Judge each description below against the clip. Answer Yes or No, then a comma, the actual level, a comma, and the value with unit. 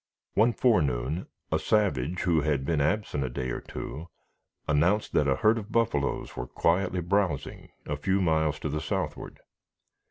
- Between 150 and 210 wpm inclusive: Yes, average, 160 wpm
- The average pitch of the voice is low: Yes, very low, 80 Hz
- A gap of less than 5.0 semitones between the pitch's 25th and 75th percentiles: No, wide, 5.6 semitones